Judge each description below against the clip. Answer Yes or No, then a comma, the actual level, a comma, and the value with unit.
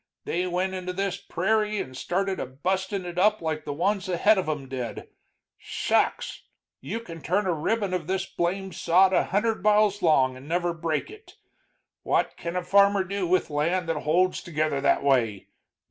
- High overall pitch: No, medium, 180 Hz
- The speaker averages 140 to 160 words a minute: No, average, 185 wpm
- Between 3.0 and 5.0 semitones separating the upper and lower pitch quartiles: Yes, average, 4.0 semitones